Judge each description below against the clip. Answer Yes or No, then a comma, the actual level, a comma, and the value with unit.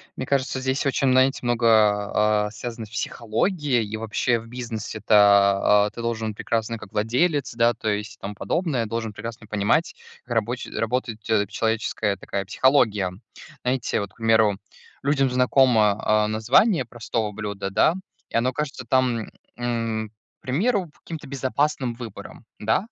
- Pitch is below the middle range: Yes, low, 115 Hz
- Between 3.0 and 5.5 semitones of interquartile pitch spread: Yes, average, 3.3 semitones